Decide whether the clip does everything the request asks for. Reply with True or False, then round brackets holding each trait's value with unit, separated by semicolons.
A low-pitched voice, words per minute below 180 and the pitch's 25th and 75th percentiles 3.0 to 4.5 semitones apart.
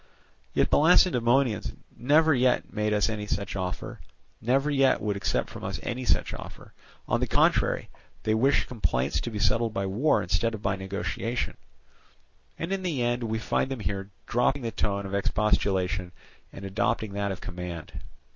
True (110 Hz; 170 wpm; 4.2 semitones)